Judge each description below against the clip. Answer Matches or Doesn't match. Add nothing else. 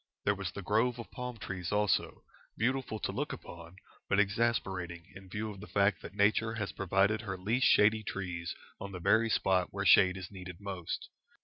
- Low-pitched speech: Matches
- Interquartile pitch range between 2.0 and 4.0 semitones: Matches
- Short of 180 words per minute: Doesn't match